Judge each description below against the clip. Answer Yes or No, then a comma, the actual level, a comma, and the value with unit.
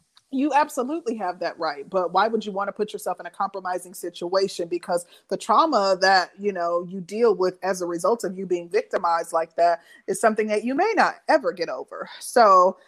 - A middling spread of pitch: Yes, average, 4.2 semitones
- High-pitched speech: Yes, high, 195 Hz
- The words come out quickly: Yes, fast, 210 wpm